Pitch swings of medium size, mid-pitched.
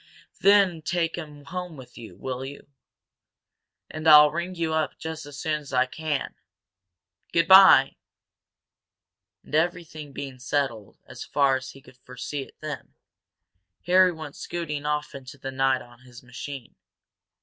Yes: average, 3.5 semitones; medium, 150 Hz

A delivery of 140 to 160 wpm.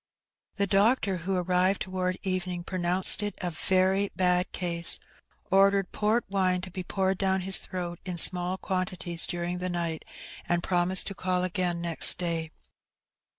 Yes: average, 150 wpm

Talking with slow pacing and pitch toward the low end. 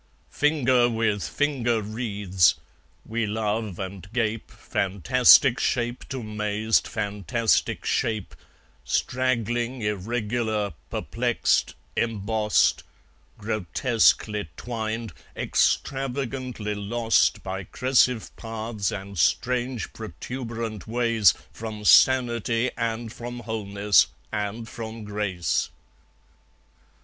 Yes: slow, 80 wpm; low, 110 Hz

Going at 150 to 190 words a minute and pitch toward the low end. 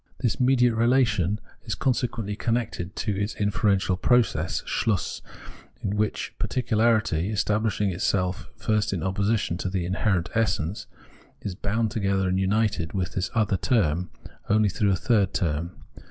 No: average, 140 wpm; low, 105 Hz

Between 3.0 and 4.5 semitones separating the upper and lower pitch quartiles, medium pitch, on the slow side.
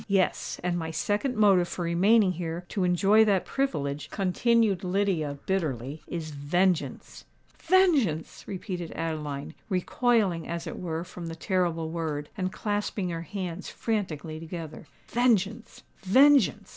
Yes: average, 3.9 semitones; medium, 180 Hz; slow, 125 wpm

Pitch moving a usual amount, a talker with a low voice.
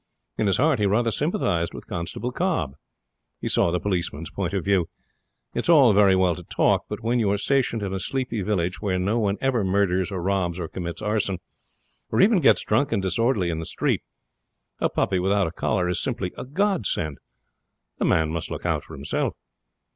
Yes: average, 4.7 semitones; low, 100 Hz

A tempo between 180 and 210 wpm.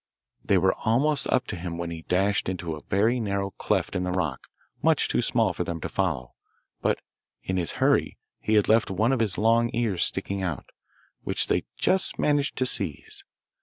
Yes: average, 195 wpm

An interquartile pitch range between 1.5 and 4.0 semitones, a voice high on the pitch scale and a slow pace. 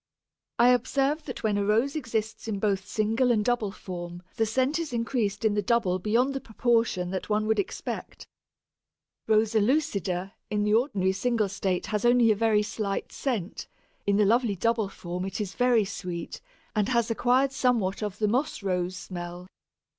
No: average, 3.5 semitones; high, 215 Hz; average, 175 wpm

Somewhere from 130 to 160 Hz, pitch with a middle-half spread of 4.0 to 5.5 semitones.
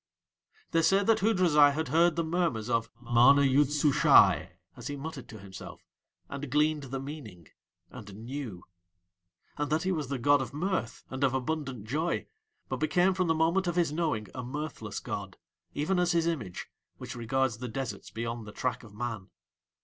Yes: medium, 140 Hz; average, 5.1 semitones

